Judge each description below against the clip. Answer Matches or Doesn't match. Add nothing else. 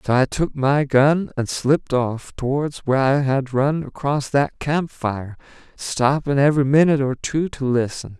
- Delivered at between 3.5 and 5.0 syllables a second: Matches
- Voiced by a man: Matches